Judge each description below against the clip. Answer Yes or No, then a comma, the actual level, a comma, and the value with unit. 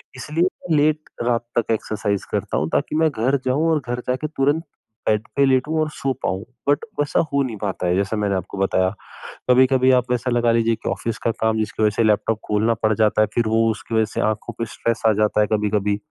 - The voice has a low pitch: Yes, low, 115 Hz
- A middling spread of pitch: Yes, average, 3.7 semitones